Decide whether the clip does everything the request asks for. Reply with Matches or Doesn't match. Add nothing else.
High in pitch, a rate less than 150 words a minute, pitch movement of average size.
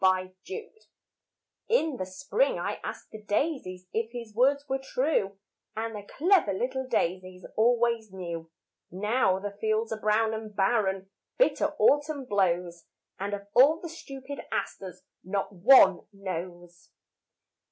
Doesn't match